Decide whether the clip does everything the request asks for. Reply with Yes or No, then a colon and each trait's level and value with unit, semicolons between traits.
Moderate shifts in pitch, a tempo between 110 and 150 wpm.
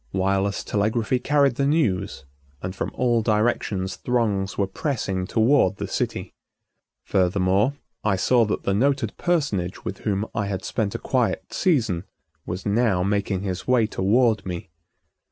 Yes: average, 4.3 semitones; average, 145 wpm